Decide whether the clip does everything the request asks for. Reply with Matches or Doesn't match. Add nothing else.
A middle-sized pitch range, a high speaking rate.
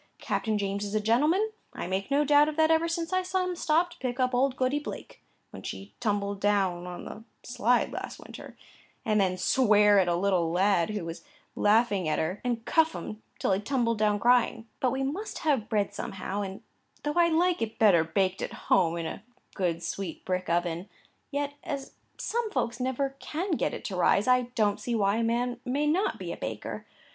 Doesn't match